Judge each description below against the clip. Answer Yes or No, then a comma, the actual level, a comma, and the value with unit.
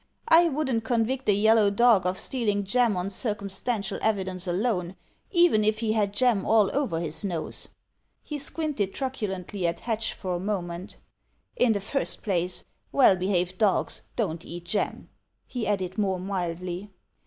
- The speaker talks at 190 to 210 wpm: No, average, 155 wpm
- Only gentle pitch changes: No, average, 3.9 semitones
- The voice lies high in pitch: Yes, high, 205 Hz